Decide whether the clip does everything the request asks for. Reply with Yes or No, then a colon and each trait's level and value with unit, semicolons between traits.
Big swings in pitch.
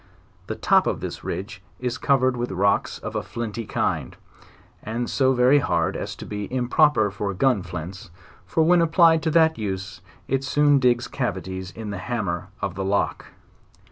Yes: wide, 5.7 semitones